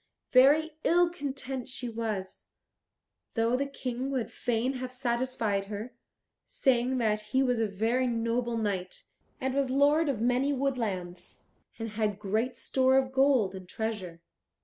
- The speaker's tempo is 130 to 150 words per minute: Yes, average, 145 wpm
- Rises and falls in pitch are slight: No, average, 3.4 semitones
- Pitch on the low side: No, high, 245 Hz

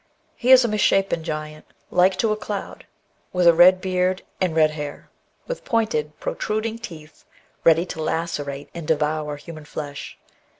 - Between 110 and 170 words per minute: Yes, average, 160 wpm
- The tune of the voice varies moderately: Yes, average, 4.2 semitones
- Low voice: No, medium, 170 Hz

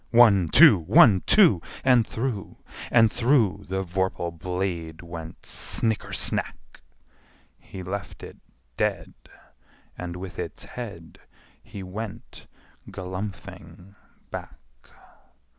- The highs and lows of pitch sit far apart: No, average, 3.8 semitones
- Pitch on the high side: No, very low, 95 Hz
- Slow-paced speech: Yes, slow, 100 wpm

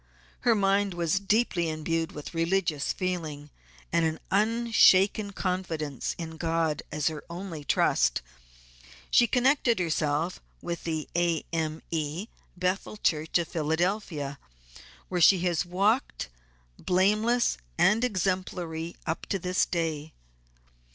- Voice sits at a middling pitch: Yes, medium, 175 Hz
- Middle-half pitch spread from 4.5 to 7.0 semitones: No, average, 3.4 semitones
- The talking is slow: Yes, slow, 110 wpm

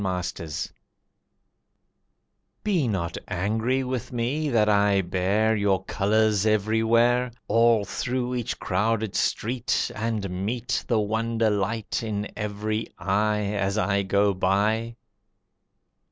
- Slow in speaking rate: Yes, slow, 110 wpm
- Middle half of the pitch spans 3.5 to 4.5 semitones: No, narrow, 2.5 semitones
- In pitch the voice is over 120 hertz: No, low, 110 Hz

